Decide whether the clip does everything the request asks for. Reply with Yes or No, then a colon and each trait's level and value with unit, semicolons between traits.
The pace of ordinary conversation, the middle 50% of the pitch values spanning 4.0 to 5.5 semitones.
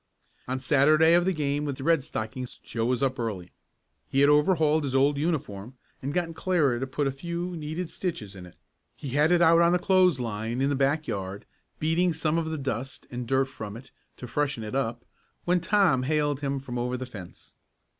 No: fast, 215 wpm; average, 4.4 semitones